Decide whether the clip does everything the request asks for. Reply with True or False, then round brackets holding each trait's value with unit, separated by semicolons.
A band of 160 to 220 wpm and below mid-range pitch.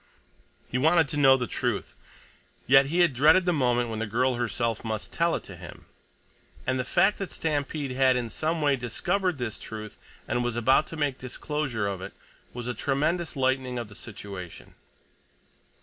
True (180 wpm; 130 Hz)